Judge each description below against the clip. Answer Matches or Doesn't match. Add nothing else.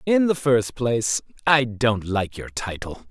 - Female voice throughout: Doesn't match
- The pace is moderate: Matches